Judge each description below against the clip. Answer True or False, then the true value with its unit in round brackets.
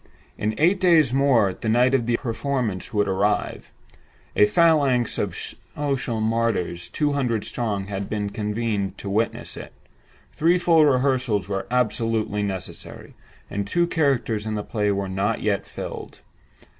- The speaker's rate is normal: True (145 wpm)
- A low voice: True (115 Hz)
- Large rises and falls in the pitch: False (4.8 semitones)